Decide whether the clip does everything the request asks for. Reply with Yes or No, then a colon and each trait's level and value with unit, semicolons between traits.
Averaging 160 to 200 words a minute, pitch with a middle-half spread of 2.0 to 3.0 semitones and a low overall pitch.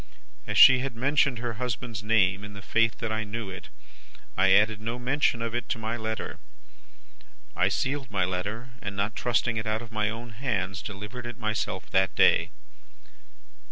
Yes: average, 180 wpm; average, 2.7 semitones; low, 110 Hz